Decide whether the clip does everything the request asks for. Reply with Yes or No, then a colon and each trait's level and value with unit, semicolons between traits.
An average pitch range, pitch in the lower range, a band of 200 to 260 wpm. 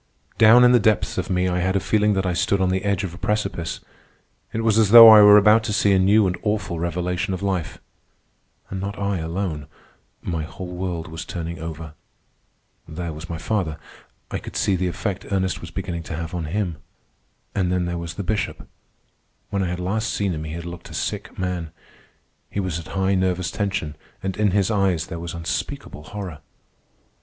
Yes: average, 3.0 semitones; very low, 95 Hz; fast, 205 wpm